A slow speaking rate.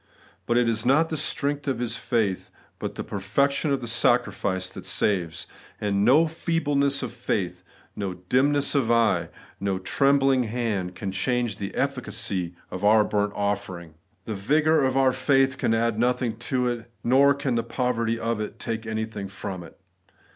No: average, 175 wpm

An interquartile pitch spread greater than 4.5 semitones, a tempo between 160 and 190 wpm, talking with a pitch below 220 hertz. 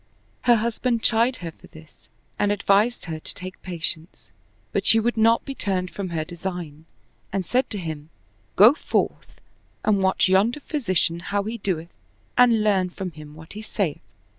Yes: average, 4.9 semitones; average, 175 wpm; high, 190 Hz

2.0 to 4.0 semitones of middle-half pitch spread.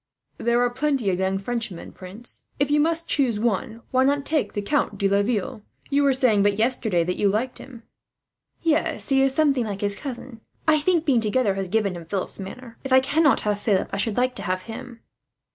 No: average, 5.0 semitones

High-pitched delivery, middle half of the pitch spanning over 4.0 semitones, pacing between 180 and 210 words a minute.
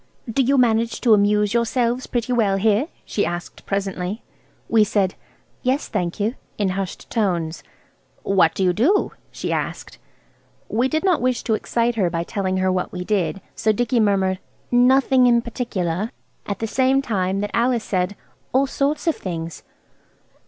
No: high, 215 Hz; average, 4.5 semitones; average, 165 wpm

